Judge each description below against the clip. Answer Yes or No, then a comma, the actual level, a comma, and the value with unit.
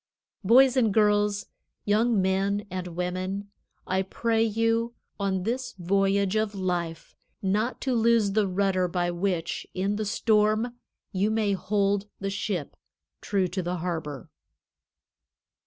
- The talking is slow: Yes, slow, 130 wpm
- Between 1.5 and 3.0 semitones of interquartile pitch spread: Yes, narrow, 2.6 semitones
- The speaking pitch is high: Yes, high, 200 Hz